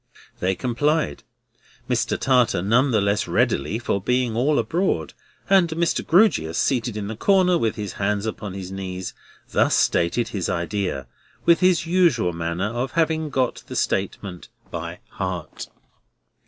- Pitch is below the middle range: Yes, low, 115 Hz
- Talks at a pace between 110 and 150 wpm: Yes, average, 145 wpm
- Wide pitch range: Yes, wide, 8.1 semitones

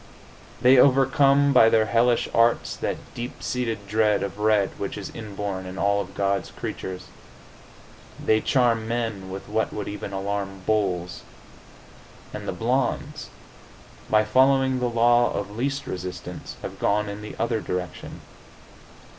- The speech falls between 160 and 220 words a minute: No, average, 140 wpm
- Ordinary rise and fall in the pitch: Yes, average, 3.3 semitones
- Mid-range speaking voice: No, low, 110 Hz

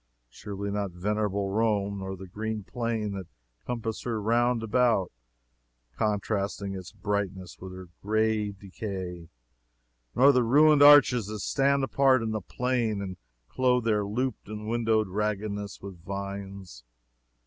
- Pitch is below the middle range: Yes, low, 105 Hz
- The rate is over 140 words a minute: No, slow, 135 wpm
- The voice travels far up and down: No, average, 2.8 semitones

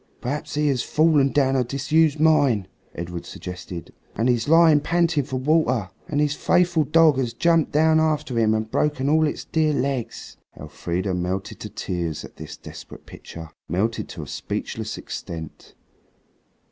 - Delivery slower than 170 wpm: Yes, average, 160 wpm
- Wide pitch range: Yes, wide, 6.2 semitones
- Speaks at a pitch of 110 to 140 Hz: Yes, low, 135 Hz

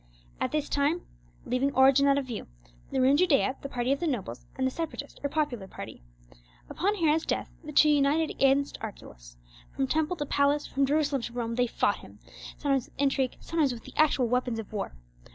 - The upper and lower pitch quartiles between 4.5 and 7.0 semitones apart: No, average, 3.1 semitones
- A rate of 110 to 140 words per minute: No, fast, 205 wpm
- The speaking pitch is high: Yes, very high, 275 Hz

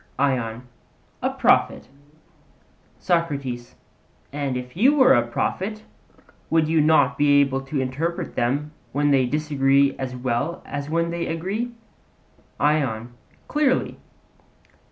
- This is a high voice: No, medium, 145 Hz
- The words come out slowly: Yes, slow, 115 wpm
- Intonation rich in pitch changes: No, average, 4.3 semitones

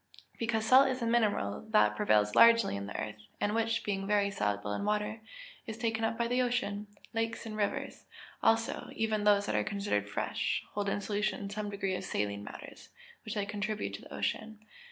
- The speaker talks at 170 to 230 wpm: Yes, average, 195 wpm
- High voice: Yes, high, 210 Hz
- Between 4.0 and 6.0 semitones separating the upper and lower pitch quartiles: No, narrow, 2.4 semitones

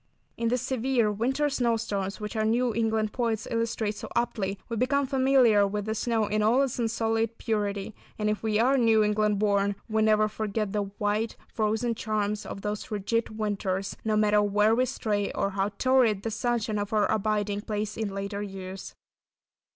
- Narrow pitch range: Yes, narrow, 1.9 semitones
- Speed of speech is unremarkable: Yes, average, 180 wpm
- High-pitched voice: Yes, high, 215 Hz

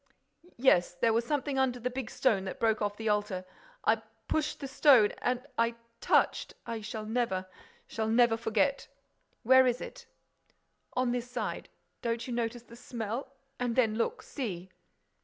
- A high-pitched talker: Yes, high, 235 Hz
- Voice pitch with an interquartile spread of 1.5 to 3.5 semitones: Yes, average, 2.9 semitones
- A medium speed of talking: No, slow, 130 wpm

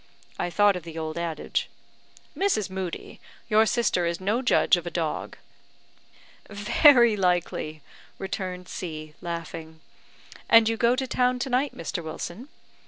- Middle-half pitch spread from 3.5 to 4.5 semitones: No, wide, 5.5 semitones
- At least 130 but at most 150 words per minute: Yes, average, 140 wpm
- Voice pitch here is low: No, medium, 185 Hz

